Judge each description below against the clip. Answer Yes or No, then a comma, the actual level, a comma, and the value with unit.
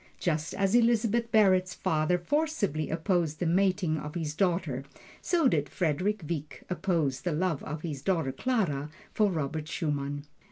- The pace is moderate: Yes, average, 150 wpm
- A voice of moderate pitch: Yes, medium, 170 Hz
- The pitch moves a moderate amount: Yes, average, 4.5 semitones